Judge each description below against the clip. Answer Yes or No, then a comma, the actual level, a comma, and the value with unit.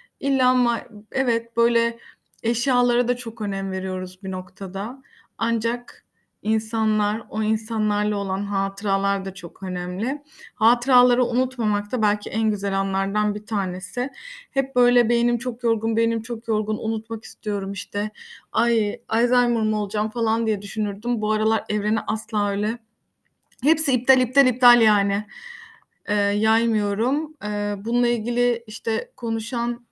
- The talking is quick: No, average, 130 wpm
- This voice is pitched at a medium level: No, high, 225 Hz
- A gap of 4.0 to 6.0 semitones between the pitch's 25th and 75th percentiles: No, average, 2.8 semitones